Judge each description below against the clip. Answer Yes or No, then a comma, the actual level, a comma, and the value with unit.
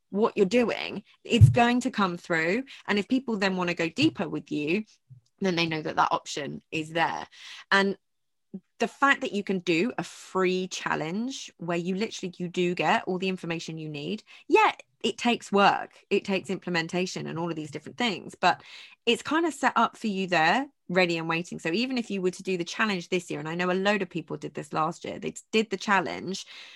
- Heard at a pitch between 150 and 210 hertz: Yes, high, 190 Hz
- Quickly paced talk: Yes, fast, 220 wpm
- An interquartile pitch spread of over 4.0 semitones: Yes, average, 4.5 semitones